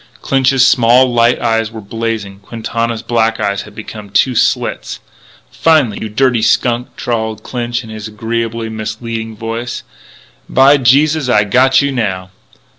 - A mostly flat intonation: Yes, narrow, 2.2 semitones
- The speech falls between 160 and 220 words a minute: No, average, 145 wpm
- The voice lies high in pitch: No, low, 115 Hz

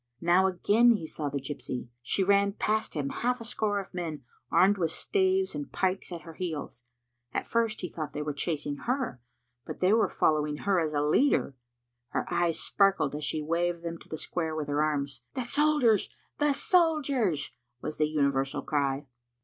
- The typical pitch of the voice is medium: Yes, medium, 170 Hz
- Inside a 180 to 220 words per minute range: Yes, average, 185 wpm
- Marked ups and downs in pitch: Yes, wide, 6.5 semitones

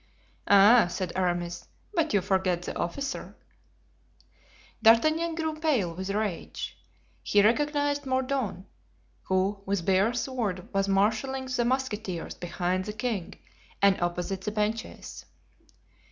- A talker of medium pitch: No, high, 210 Hz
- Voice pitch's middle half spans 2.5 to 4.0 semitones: No, wide, 5.6 semitones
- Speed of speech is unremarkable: No, slow, 115 wpm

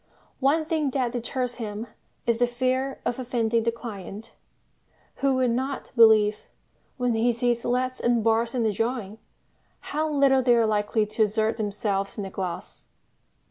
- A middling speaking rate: Yes, average, 160 wpm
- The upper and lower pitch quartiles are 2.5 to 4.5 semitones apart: Yes, average, 2.8 semitones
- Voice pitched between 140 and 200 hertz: No, high, 235 Hz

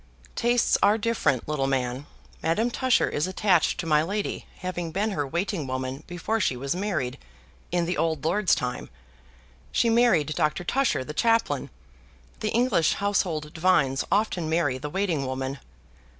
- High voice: No, medium, 165 Hz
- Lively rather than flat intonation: Yes, wide, 6.3 semitones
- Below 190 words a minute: Yes, average, 150 wpm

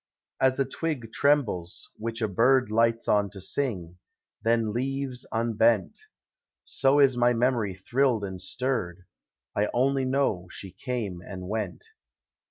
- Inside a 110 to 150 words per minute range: Yes, average, 140 wpm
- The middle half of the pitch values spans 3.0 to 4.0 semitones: No, average, 4.8 semitones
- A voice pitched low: Yes, low, 115 Hz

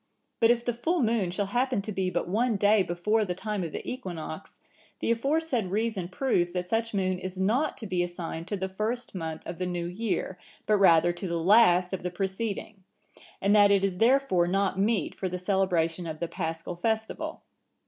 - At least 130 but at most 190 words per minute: No, average, 200 wpm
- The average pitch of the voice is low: No, high, 190 Hz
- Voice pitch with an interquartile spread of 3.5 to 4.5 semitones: Yes, average, 3.9 semitones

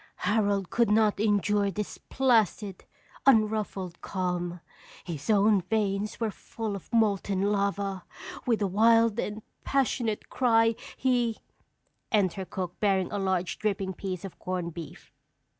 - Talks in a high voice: Yes, high, 205 Hz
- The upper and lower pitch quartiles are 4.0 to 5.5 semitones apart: No, average, 2.7 semitones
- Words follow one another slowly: Yes, slow, 130 wpm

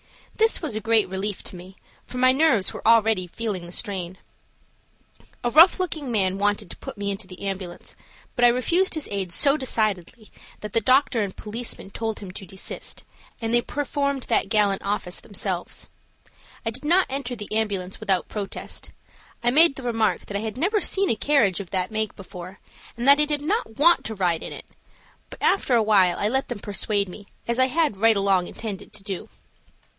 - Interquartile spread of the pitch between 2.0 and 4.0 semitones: No, average, 4.9 semitones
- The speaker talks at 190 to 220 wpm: Yes, average, 195 wpm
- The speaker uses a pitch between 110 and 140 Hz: No, high, 215 Hz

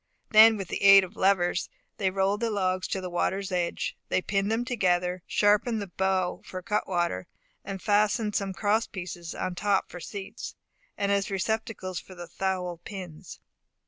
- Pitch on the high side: Yes, high, 195 Hz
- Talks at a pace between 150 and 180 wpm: Yes, average, 175 wpm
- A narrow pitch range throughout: Yes, narrow, 2.2 semitones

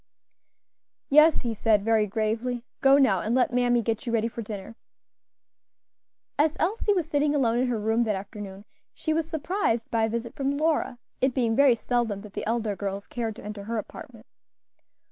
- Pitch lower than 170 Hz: No, high, 235 Hz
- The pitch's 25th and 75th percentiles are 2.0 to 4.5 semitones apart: Yes, average, 4.1 semitones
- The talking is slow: No, average, 185 wpm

